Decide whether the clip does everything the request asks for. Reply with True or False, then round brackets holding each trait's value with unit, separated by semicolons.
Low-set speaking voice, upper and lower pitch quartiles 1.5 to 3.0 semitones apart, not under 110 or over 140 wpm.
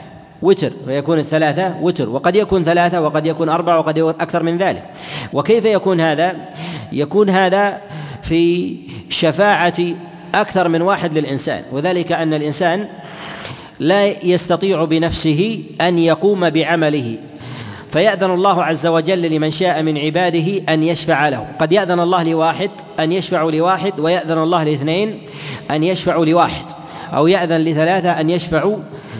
False (170 Hz; 2.5 semitones; 130 wpm)